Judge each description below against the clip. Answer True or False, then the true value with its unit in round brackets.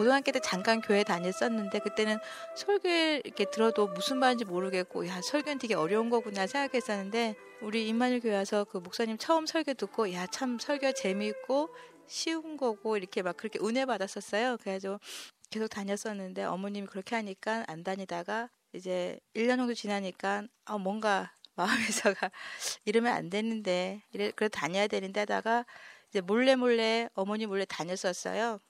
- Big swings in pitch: False (3.7 semitones)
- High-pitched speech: True (215 Hz)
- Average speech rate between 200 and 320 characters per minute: False (360 characters per minute)